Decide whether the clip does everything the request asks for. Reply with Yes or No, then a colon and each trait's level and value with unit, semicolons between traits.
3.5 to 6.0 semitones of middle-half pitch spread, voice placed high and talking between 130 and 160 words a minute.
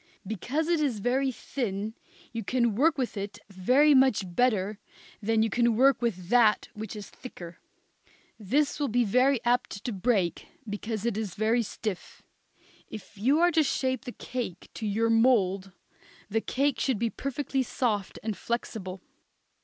Yes: average, 4.0 semitones; high, 230 Hz; average, 155 wpm